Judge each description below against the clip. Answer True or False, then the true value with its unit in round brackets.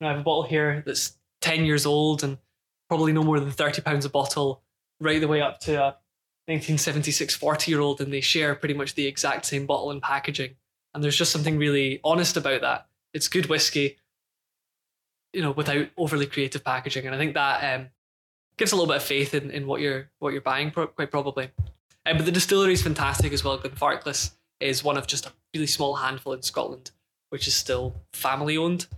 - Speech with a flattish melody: True (2.2 semitones)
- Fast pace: True (215 wpm)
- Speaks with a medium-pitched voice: True (145 Hz)